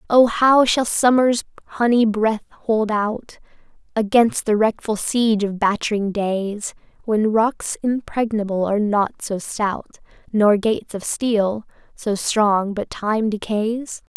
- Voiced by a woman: Yes, female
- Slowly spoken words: Yes, slow, 130 wpm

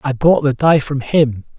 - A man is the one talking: Yes, male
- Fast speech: Yes, fast, 225 wpm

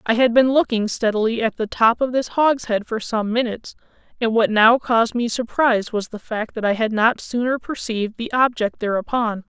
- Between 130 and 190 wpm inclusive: No, average, 200 wpm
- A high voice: Yes, high, 230 Hz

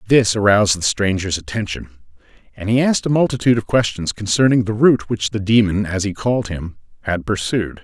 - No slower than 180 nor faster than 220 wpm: Yes, average, 185 wpm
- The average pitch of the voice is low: Yes, low, 105 Hz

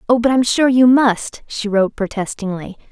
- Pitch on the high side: Yes, high, 225 Hz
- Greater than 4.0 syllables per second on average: Yes, 5.5 syllables/s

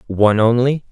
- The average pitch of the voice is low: Yes, low, 120 Hz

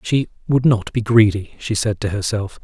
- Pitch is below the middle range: Yes, low, 110 Hz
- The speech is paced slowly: No, fast, 205 wpm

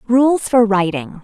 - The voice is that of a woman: Yes, female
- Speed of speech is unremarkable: Yes, average, 145 wpm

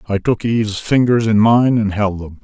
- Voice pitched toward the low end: Yes, low, 110 Hz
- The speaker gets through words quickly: Yes, fast, 220 wpm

